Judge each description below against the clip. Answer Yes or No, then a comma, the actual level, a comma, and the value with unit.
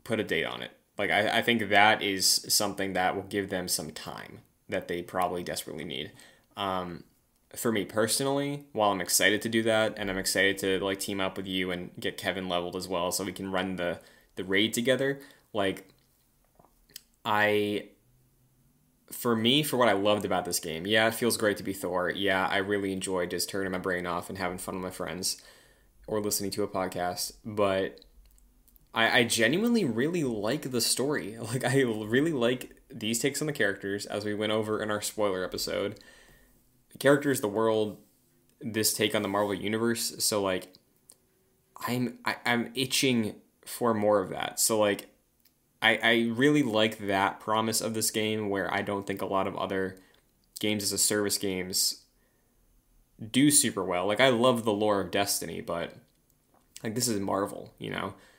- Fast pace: No, average, 185 wpm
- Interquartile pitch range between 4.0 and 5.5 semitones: No, average, 3.3 semitones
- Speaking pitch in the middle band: No, low, 105 Hz